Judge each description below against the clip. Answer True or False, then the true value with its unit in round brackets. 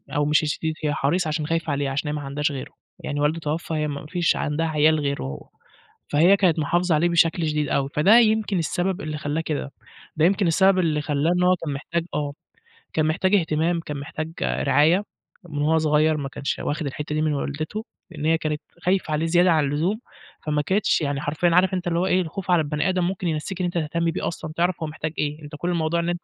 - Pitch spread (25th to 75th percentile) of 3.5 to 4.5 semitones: False (2.8 semitones)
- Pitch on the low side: False (155 Hz)